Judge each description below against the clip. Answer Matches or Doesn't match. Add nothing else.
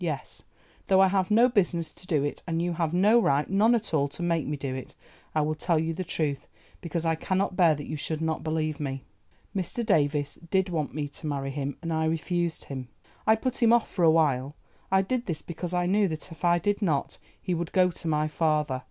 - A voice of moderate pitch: Matches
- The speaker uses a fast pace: Matches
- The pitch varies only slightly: Doesn't match